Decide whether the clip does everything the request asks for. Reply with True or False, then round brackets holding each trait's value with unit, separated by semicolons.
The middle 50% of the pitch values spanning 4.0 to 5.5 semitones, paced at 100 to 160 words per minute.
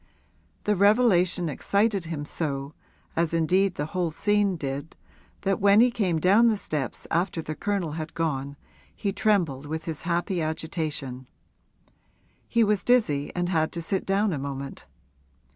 True (4.5 semitones; 150 wpm)